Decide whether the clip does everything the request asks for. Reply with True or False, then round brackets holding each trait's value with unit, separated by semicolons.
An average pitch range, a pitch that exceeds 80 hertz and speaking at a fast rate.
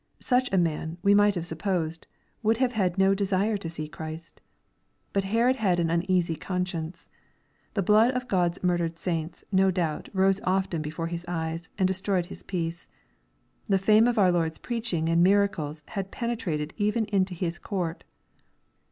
False (3.3 semitones; 185 Hz; 170 wpm)